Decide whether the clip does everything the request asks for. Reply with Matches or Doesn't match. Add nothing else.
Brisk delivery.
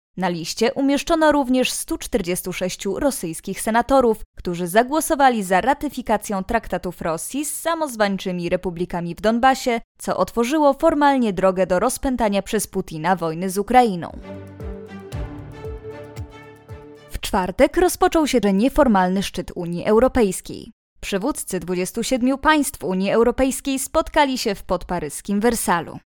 Doesn't match